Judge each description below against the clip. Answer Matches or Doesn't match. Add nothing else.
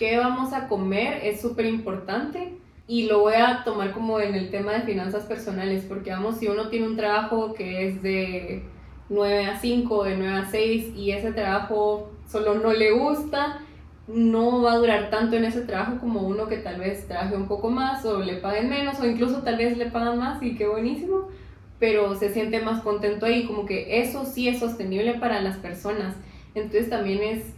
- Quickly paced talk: Matches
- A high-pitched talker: Matches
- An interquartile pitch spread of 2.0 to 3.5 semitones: Matches